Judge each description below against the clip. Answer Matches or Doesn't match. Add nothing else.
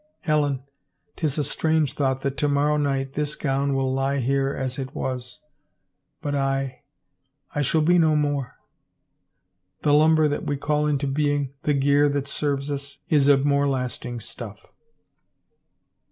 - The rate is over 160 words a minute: Doesn't match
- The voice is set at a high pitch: Doesn't match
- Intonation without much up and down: Matches